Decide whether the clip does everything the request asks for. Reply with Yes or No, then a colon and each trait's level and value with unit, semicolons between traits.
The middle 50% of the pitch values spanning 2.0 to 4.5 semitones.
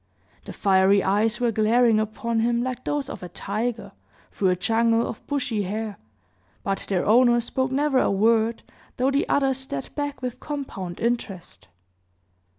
Yes: average, 4.0 semitones